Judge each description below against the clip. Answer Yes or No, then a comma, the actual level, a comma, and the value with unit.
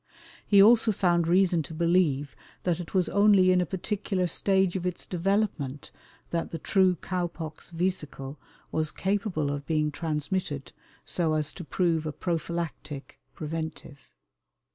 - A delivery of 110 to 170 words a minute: Yes, average, 140 wpm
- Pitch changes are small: No, average, 3.3 semitones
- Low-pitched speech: No, medium, 170 Hz